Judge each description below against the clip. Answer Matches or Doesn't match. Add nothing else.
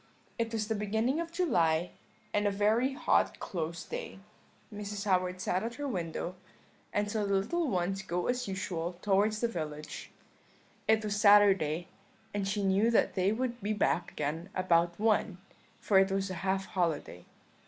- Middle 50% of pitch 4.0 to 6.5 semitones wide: Doesn't match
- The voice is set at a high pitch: Matches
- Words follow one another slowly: Doesn't match